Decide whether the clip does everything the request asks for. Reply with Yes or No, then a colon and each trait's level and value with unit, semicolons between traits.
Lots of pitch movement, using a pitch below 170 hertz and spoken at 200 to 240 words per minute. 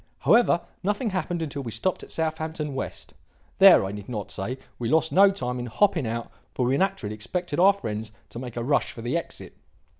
Yes: wide, 7.1 semitones; medium, 140 Hz; fast, 205 wpm